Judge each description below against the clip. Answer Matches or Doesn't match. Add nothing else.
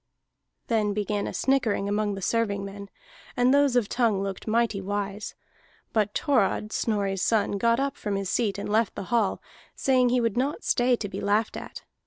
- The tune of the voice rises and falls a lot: Doesn't match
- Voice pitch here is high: Matches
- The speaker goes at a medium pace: Matches